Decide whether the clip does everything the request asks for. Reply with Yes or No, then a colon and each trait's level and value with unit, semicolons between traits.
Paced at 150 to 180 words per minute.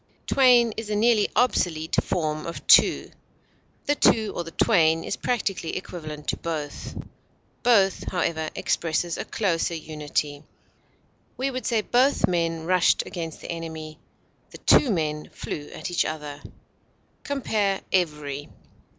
No: slow, 135 wpm